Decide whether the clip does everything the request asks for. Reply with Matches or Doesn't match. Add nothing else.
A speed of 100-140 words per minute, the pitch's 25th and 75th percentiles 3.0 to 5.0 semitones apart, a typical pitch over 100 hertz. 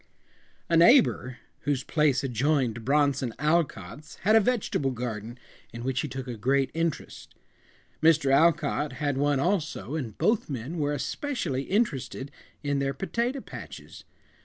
Matches